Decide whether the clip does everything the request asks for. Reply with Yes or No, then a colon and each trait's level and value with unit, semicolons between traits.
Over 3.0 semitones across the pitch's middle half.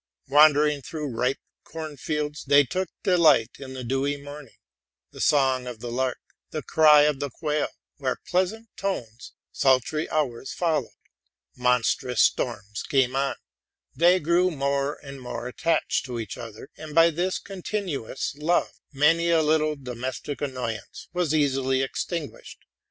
Yes: average, 3.5 semitones